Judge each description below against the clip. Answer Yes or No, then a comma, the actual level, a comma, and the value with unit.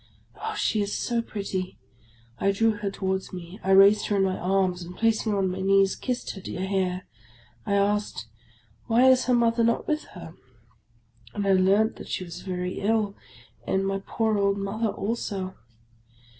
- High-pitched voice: Yes, high, 195 Hz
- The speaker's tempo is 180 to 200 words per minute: Yes, average, 185 wpm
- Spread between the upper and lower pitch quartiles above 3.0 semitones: No, average, 2.7 semitones